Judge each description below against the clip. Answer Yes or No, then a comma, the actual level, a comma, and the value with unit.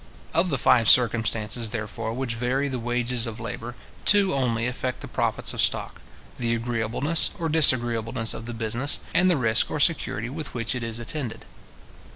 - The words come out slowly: No, average, 175 wpm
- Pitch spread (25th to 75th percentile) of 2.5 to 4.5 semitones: Yes, average, 2.8 semitones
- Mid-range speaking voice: No, low, 120 Hz